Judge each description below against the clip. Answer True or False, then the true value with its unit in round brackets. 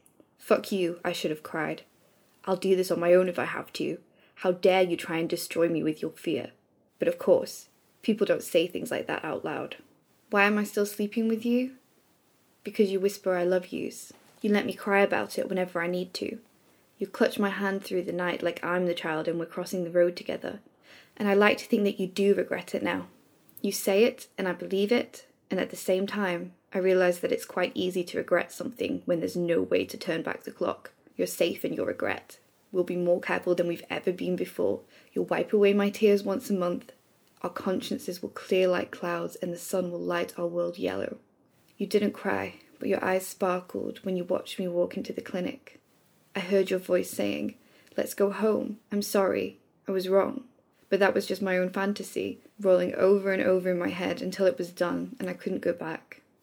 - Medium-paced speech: False (220 wpm)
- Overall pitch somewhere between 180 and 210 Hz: True (190 Hz)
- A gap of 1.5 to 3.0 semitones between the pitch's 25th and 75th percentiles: True (2.4 semitones)